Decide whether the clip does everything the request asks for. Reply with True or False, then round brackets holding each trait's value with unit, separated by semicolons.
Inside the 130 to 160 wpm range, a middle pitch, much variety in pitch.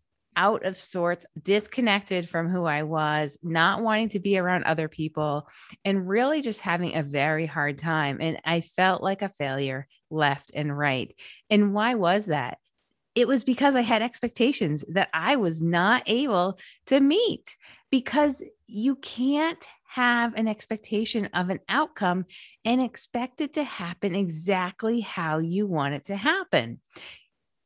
False (150 wpm; 195 Hz; 6.5 semitones)